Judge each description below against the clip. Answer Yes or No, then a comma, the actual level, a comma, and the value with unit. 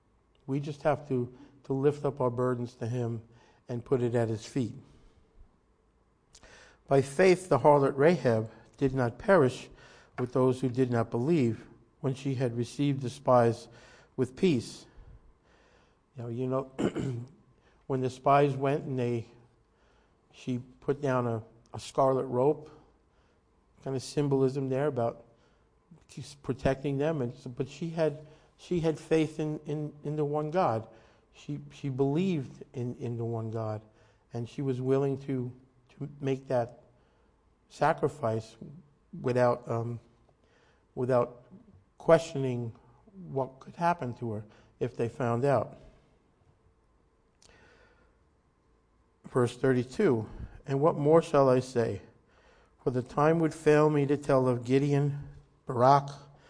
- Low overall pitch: Yes, low, 130 Hz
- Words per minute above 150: No, slow, 135 wpm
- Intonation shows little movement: No, average, 3.3 semitones